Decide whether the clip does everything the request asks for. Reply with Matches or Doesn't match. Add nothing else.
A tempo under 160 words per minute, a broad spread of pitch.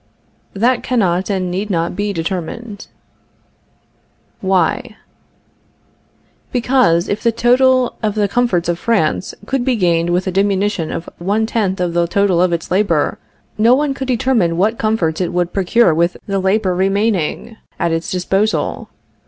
Doesn't match